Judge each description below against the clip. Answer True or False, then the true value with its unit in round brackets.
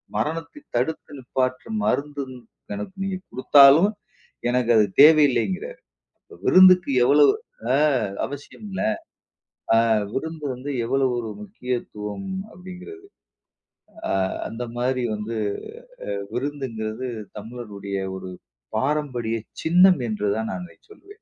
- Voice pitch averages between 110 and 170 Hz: True (135 Hz)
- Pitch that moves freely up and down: True (6.0 semitones)